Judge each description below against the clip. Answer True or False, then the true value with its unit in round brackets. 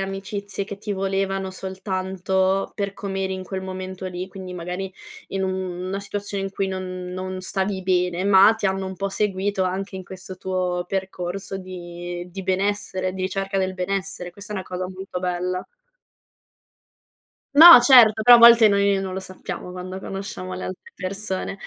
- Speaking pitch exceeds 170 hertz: True (190 Hz)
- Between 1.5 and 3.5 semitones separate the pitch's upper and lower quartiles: False (1.1 semitones)